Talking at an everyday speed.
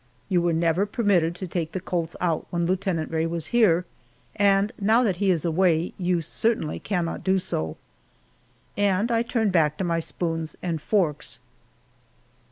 Yes: average, 165 wpm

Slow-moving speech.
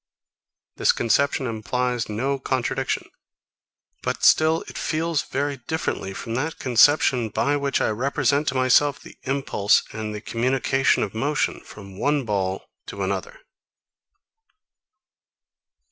Yes: slow, 120 wpm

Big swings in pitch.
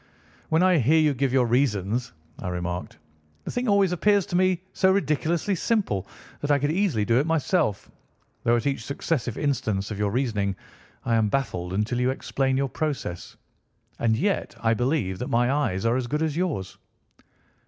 Yes: wide, 6.4 semitones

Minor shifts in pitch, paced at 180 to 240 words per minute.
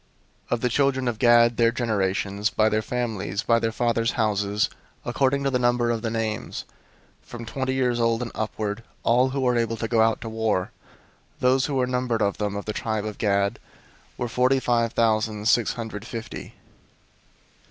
Yes: narrow, 2.2 semitones; average, 190 wpm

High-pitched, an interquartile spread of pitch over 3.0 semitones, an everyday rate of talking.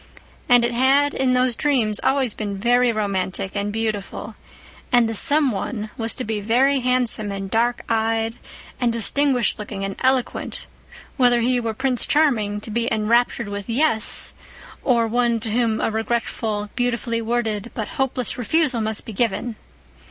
No: high, 230 Hz; narrow, 2.6 semitones; average, 160 wpm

